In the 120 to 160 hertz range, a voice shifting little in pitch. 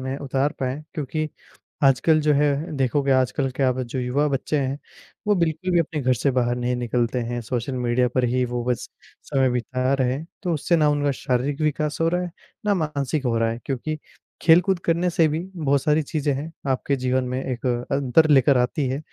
No: low, 135 Hz; average, 3.3 semitones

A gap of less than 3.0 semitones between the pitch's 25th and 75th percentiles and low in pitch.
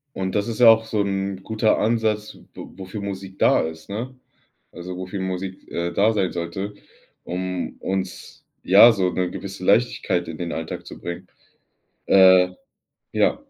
Yes: narrow, 2.4 semitones; very low, 95 Hz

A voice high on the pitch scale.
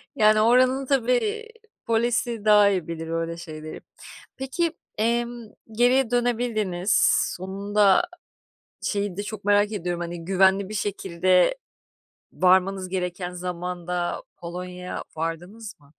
Yes: high, 200 Hz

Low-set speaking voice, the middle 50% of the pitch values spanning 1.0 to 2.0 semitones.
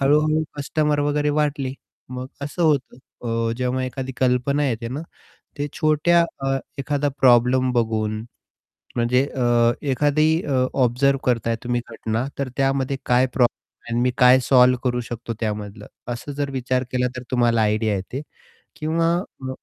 No: low, 130 Hz; average, 2.9 semitones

